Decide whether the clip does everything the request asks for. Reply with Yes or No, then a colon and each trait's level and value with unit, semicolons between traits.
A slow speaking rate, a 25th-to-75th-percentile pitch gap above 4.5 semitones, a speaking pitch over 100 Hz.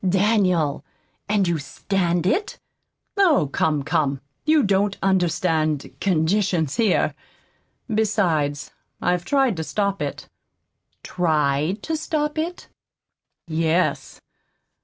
Yes: slow, 95 wpm; average, 5.0 semitones; medium, 185 Hz